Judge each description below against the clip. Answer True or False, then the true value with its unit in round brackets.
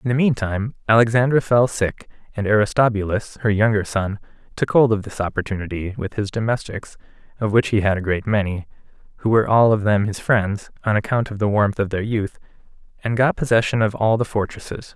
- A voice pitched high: False (110 Hz)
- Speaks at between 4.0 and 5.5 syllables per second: False (5.7 syllables/s)